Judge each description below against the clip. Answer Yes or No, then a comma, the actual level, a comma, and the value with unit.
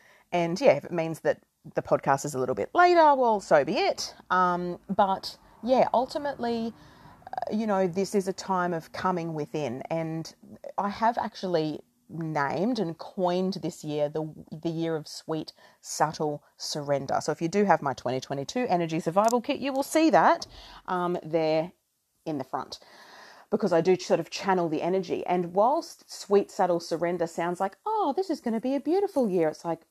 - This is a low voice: No, medium, 180 Hz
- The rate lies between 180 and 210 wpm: Yes, average, 185 wpm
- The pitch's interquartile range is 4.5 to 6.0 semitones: Yes, average, 5.1 semitones